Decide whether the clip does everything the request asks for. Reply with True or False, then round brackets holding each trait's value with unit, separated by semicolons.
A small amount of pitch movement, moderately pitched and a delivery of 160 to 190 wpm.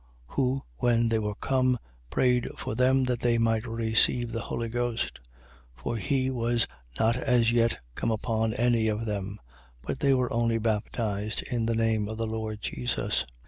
False (1.8 semitones; 115 Hz; 180 wpm)